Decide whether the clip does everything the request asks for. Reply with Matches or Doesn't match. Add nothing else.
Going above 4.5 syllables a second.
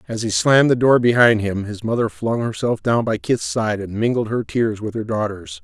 Matches